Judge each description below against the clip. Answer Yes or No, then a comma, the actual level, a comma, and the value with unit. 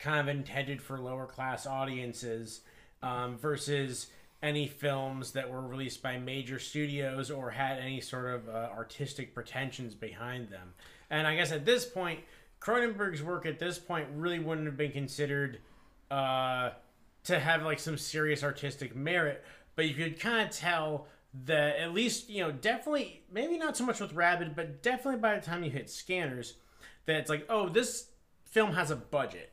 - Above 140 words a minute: Yes, average, 175 wpm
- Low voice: No, medium, 145 Hz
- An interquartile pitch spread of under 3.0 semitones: No, average, 5.0 semitones